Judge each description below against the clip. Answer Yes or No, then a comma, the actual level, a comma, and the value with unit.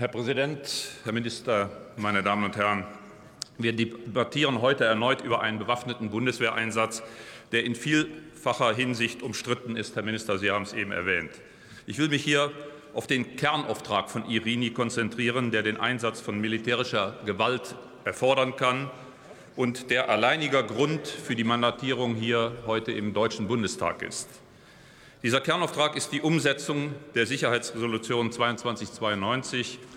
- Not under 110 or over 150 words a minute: Yes, average, 135 wpm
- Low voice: Yes, low, 120 Hz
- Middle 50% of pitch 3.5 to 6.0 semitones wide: No, average, 3.0 semitones